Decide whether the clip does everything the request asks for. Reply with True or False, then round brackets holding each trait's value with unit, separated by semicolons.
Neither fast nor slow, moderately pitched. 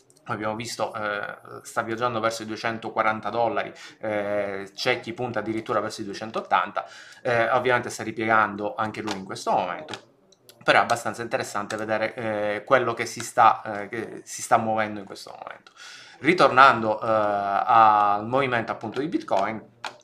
False (155 wpm; 110 Hz)